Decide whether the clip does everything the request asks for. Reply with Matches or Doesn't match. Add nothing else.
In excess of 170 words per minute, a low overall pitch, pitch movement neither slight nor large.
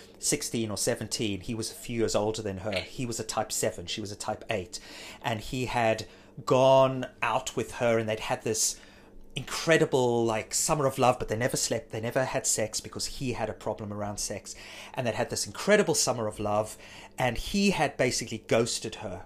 Matches